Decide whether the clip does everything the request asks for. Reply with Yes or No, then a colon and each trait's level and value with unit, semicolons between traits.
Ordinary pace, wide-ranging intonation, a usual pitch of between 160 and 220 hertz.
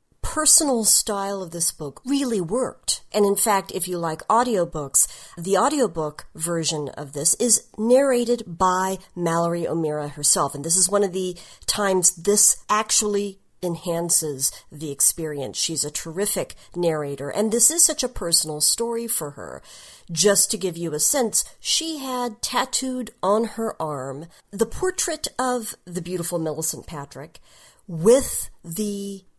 Yes: average, 145 wpm; wide, 5.8 semitones; medium, 185 Hz